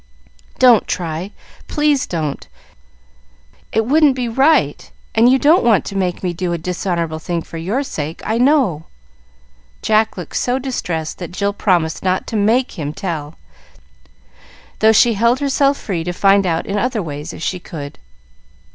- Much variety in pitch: Yes, wide, 6.5 semitones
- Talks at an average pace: Yes, average, 160 wpm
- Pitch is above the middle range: Yes, high, 195 Hz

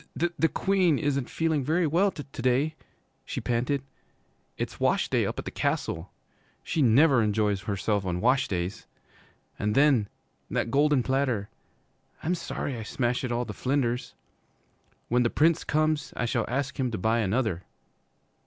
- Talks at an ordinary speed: Yes, average, 160 wpm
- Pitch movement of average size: Yes, average, 4.9 semitones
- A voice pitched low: Yes, low, 125 Hz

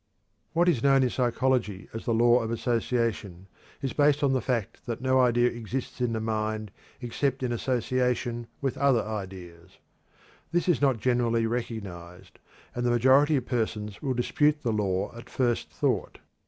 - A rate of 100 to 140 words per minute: No, average, 165 wpm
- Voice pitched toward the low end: Yes, low, 120 Hz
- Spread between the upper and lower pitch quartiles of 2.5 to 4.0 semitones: Yes, average, 3.0 semitones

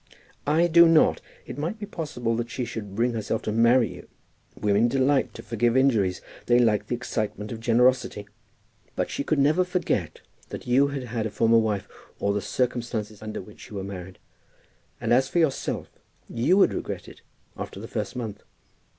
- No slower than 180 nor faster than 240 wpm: Yes, average, 185 wpm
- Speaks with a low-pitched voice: Yes, low, 120 Hz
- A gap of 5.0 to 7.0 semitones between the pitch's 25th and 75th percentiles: No, average, 4.1 semitones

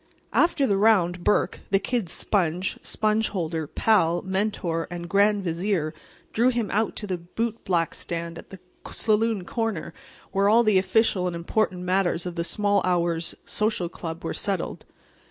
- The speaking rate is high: No, average, 155 wpm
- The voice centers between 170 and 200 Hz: Yes, high, 190 Hz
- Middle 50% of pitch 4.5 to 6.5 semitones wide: No, average, 3.7 semitones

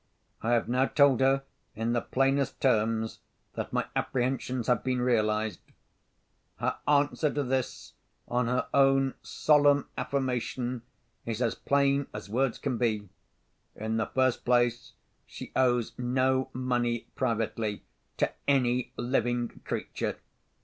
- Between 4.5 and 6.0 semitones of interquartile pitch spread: No, narrow, 2.4 semitones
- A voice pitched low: Yes, low, 125 Hz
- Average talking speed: No, slow, 130 wpm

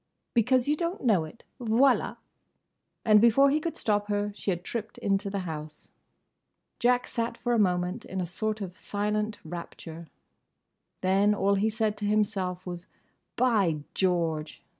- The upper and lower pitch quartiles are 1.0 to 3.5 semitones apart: No, average, 4.0 semitones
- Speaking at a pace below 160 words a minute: Yes, average, 150 wpm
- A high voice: Yes, high, 205 Hz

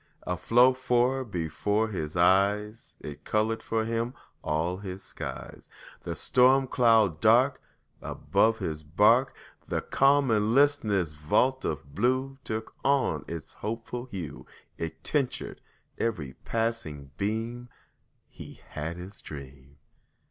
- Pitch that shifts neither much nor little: No, wide, 6.6 semitones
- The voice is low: Yes, low, 110 Hz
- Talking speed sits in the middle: No, slow, 120 wpm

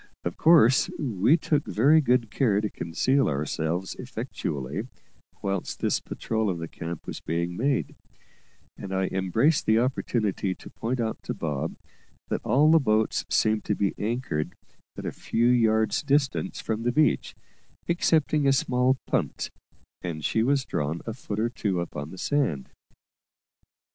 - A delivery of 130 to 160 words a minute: Yes, average, 155 wpm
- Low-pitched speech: Yes, low, 110 Hz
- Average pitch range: No, wide, 6.5 semitones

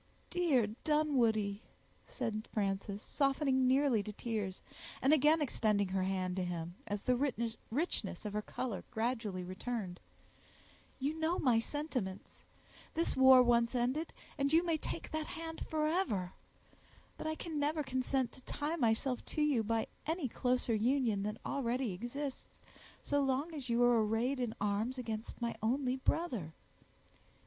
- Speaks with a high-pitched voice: Yes, high, 245 Hz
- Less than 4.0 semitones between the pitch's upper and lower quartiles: No, average, 5.0 semitones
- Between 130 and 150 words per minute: Yes, average, 140 wpm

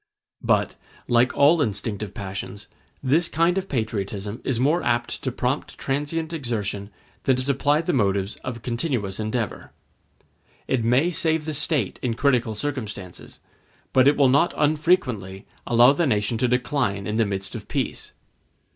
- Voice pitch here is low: Yes, low, 125 Hz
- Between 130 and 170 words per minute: Yes, average, 150 wpm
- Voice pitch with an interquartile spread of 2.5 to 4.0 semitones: No, wide, 5.5 semitones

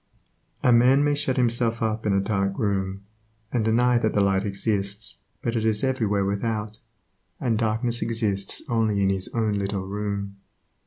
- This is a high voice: No, low, 110 Hz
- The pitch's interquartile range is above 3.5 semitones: No, average, 2.8 semitones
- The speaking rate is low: No, average, 165 wpm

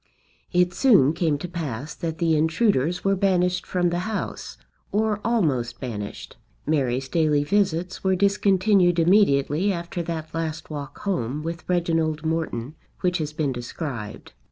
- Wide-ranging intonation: No, average, 3.8 semitones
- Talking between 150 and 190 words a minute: No, average, 140 wpm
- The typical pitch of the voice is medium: Yes, medium, 165 Hz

